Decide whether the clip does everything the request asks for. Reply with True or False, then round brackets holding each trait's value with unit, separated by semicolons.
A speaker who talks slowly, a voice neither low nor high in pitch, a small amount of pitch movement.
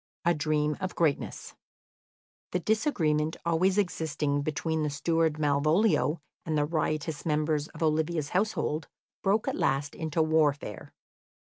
True (125 wpm; 155 Hz; 2.1 semitones)